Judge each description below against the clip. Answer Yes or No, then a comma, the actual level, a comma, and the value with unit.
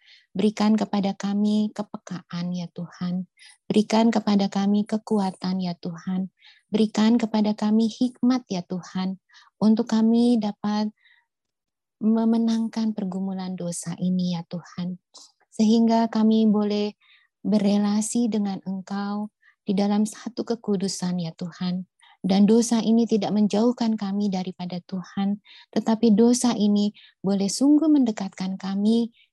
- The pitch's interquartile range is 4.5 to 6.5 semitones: No, average, 2.9 semitones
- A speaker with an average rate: Yes, average, 110 wpm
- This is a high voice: Yes, high, 210 Hz